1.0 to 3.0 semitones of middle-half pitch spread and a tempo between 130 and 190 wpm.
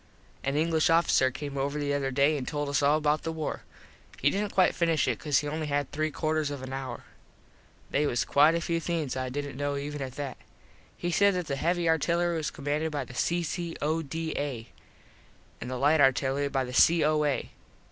No: narrow, 2.6 semitones; average, 200 wpm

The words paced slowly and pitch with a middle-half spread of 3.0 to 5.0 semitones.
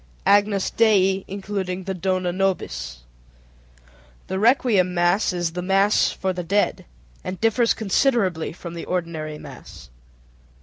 No: slow, 130 wpm; narrow, 2.5 semitones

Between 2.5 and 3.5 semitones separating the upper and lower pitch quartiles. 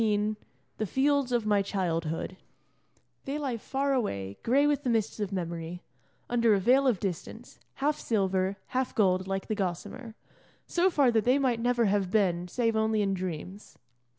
No: average, 4.8 semitones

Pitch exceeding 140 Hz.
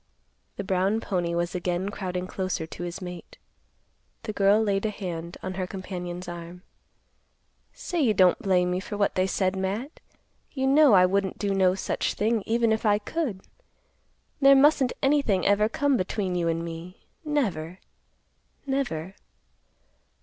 Yes: high, 190 Hz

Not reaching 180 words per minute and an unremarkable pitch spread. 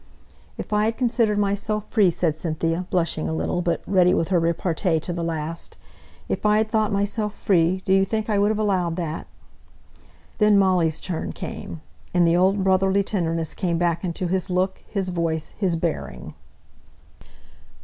Yes: average, 170 wpm; average, 3.3 semitones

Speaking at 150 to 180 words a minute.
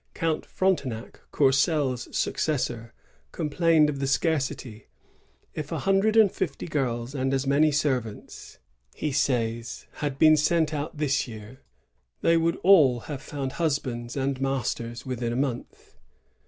No: average, 140 wpm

